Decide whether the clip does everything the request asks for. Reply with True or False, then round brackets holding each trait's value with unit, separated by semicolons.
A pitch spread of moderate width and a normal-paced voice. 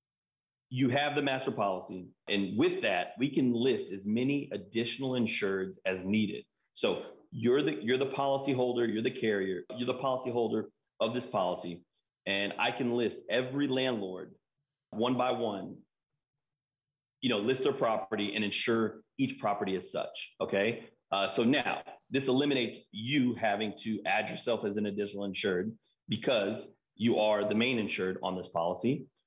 True (4.3 semitones; 160 wpm)